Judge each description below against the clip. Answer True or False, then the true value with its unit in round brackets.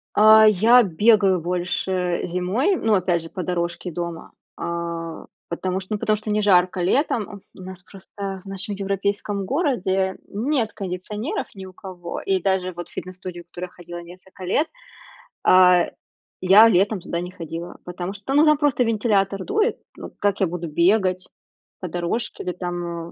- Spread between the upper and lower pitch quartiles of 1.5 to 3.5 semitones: True (2.9 semitones)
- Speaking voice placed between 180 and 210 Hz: True (190 Hz)